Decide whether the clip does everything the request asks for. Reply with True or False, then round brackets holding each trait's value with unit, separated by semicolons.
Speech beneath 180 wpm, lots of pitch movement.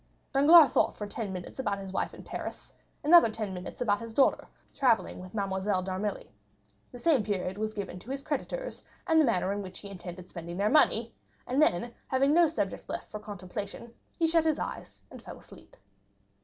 False (195 wpm; 6.3 semitones)